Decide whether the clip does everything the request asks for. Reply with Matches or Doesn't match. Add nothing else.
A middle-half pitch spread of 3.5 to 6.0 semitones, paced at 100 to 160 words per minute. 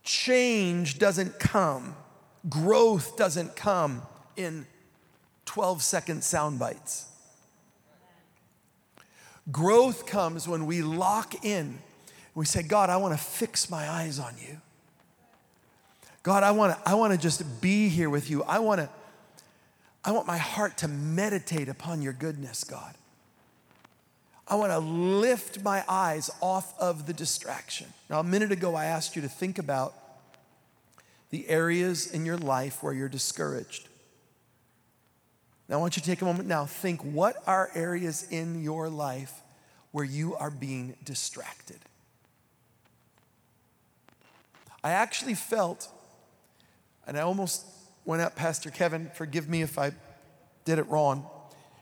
Matches